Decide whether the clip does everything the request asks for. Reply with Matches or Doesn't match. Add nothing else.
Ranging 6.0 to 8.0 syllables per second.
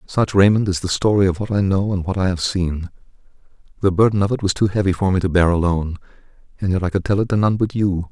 Matches